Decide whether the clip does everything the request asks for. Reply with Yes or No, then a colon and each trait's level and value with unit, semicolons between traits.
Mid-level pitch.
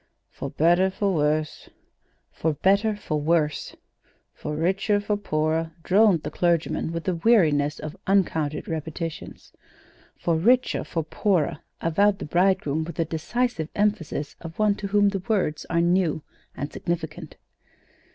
Yes: medium, 170 Hz